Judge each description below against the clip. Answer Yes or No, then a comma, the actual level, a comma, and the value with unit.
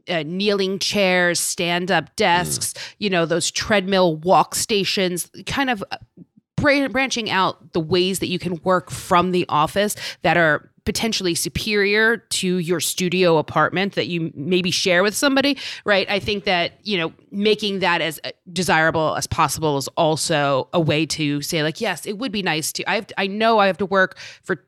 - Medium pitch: Yes, medium, 180 Hz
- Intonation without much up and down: No, average, 3.5 semitones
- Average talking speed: Yes, average, 180 wpm